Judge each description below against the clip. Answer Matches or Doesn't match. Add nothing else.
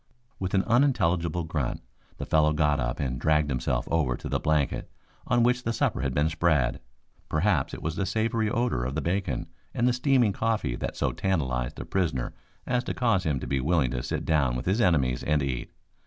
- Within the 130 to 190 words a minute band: Doesn't match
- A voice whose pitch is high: Doesn't match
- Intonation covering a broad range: Matches